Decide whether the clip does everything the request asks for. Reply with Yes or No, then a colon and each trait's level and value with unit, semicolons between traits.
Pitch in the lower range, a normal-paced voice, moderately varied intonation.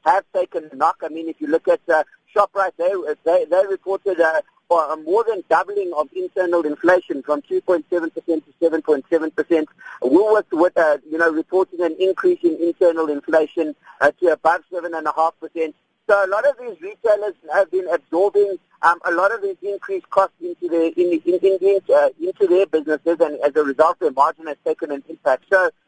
No: medium, 175 Hz; average, 195 wpm; average, 4.0 semitones